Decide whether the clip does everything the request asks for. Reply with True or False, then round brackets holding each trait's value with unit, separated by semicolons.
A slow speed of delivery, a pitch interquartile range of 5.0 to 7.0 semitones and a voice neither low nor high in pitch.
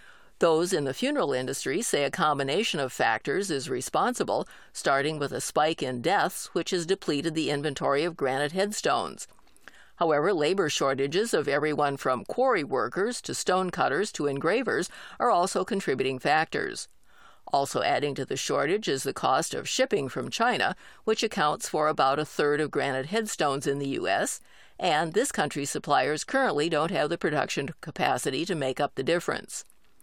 False (165 wpm; 5.4 semitones; 155 Hz)